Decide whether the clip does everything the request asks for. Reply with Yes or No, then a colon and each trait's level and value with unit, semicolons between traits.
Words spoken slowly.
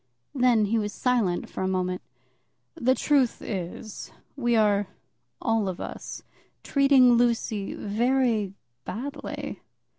Yes: slow, 115 wpm